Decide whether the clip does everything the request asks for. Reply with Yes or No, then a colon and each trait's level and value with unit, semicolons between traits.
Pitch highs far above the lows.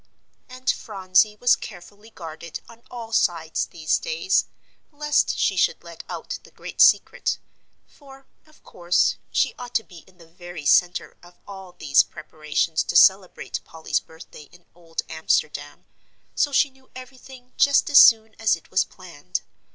Yes: wide, 7.2 semitones